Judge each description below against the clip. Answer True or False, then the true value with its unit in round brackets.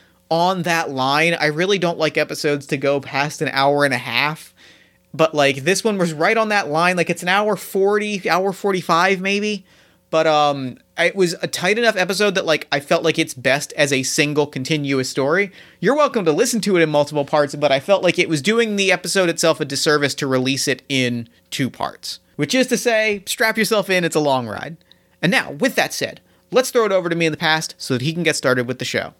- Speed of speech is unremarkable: False (235 wpm)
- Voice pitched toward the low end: False (160 Hz)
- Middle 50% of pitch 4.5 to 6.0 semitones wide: True (5.2 semitones)